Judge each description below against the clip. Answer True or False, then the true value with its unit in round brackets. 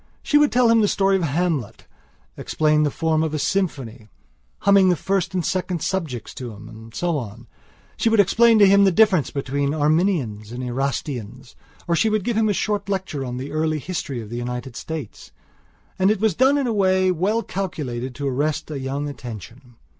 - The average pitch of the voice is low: False (155 Hz)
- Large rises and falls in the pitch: True (7.0 semitones)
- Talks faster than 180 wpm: True (200 wpm)